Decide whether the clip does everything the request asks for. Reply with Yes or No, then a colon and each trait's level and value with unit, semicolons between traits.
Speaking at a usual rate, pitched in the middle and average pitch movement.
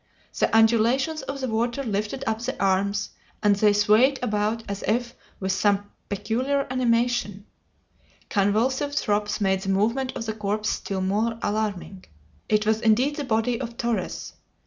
No: average, 150 wpm; high, 220 Hz; average, 3.1 semitones